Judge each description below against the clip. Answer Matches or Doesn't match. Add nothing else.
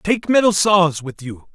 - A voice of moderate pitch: Matches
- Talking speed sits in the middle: Matches